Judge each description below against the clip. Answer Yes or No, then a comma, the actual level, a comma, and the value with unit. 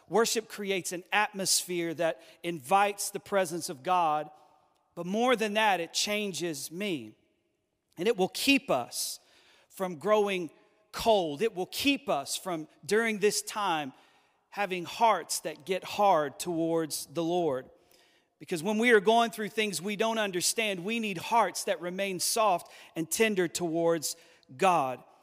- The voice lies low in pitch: No, medium, 185 Hz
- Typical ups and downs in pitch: Yes, average, 3.9 semitones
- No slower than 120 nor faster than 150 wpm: Yes, average, 145 wpm